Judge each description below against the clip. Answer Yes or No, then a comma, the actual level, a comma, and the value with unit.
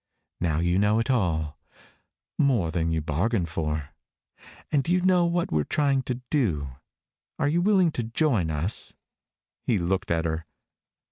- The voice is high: No, very low, 95 Hz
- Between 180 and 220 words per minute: No, average, 150 wpm